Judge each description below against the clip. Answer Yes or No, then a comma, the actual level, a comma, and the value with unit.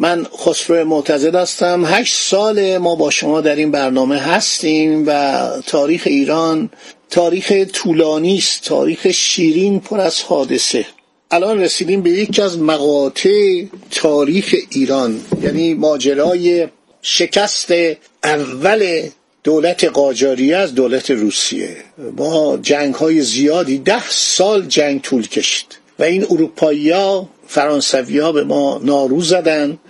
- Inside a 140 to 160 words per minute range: No, average, 120 wpm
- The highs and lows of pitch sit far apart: No, average, 4.6 semitones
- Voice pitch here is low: No, medium, 160 Hz